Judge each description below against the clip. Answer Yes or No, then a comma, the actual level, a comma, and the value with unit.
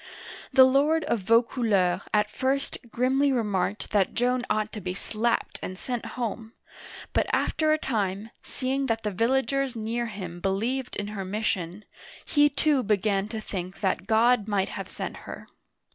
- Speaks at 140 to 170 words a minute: Yes, average, 160 wpm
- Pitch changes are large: No, average, 4.3 semitones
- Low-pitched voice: No, high, 225 Hz